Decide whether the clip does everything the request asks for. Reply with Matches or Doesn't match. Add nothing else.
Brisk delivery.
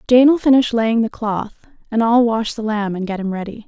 Matches